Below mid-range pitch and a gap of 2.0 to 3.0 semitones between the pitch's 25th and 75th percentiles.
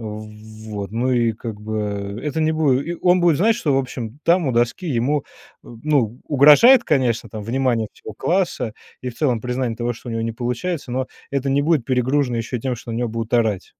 No: low, 125 Hz; average, 4.0 semitones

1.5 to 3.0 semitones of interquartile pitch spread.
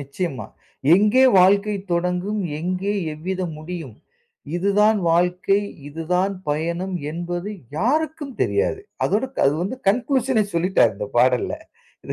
No: average, 3.8 semitones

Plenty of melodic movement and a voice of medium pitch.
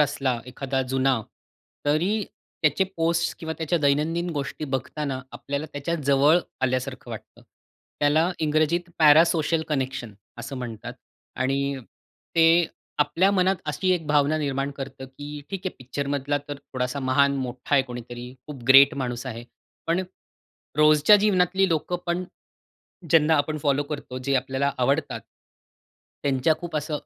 No: average, 3.3 semitones; medium, 145 Hz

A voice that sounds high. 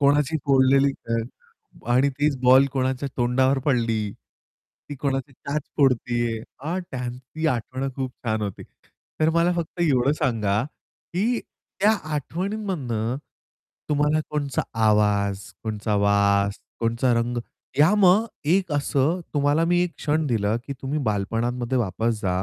No: low, 130 Hz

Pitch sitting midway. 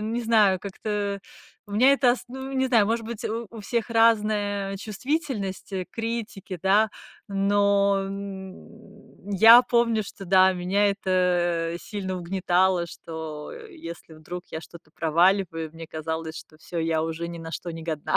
No: high, 195 Hz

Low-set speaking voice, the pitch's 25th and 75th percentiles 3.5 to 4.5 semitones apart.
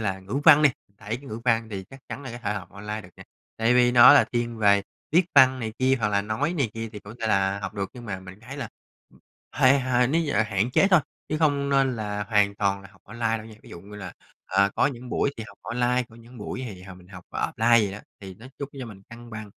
Yes: low, 115 Hz; average, 4.0 semitones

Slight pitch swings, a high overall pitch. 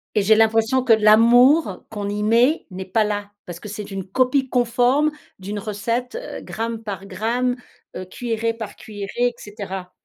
No: average, 3.1 semitones; high, 220 Hz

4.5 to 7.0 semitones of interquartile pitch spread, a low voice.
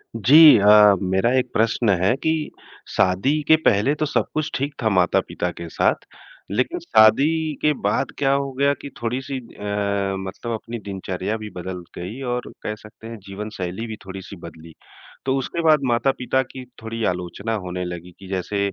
Yes: wide, 5.4 semitones; low, 110 Hz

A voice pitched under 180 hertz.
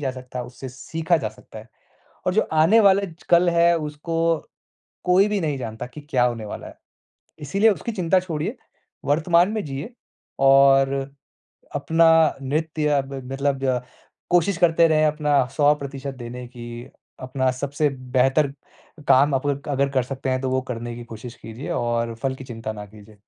Yes: medium, 140 Hz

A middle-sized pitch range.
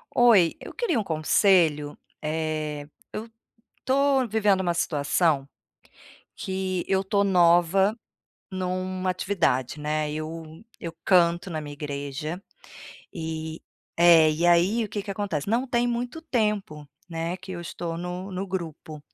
Yes: average, 4.0 semitones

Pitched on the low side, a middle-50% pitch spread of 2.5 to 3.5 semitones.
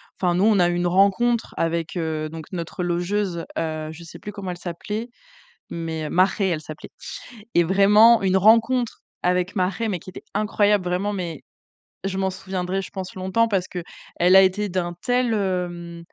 No: medium, 185 Hz; average, 2.8 semitones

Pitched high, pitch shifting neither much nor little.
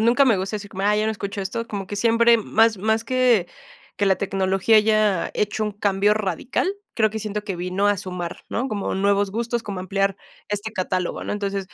No: high, 205 Hz; narrow, 2.2 semitones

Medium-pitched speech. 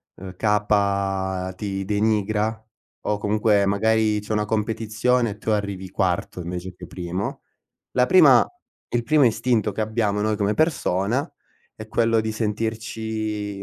No: low, 105 Hz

